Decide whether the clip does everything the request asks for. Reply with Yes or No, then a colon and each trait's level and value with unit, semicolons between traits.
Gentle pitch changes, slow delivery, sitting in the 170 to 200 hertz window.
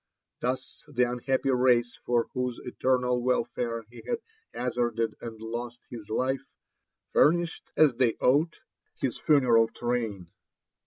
No: narrow, 1.8 semitones; slow, 120 wpm; low, 125 Hz